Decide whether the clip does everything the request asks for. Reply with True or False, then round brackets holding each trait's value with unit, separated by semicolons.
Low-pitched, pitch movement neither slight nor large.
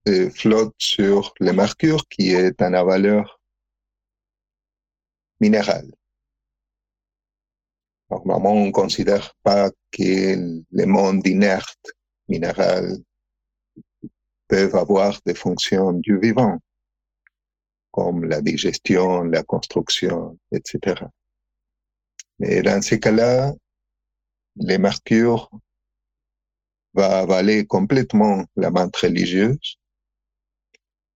False (95 Hz; 8.2 semitones)